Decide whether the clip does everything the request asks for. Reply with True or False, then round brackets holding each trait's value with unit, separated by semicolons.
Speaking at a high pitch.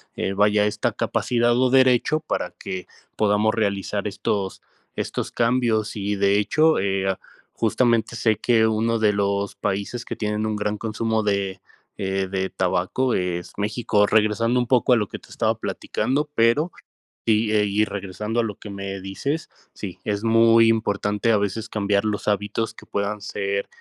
False (105 Hz)